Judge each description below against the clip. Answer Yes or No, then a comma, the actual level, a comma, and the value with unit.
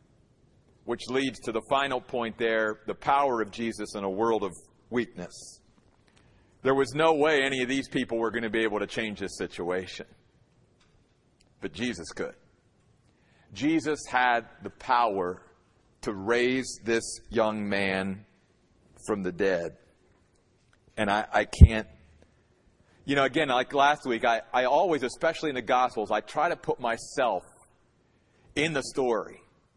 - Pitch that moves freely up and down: No, average, 4.0 semitones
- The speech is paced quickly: No, average, 145 wpm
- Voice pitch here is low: Yes, low, 115 Hz